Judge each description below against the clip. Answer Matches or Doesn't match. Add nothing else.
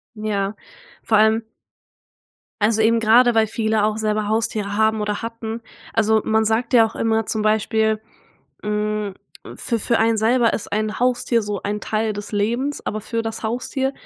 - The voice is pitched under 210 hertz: Doesn't match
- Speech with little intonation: Matches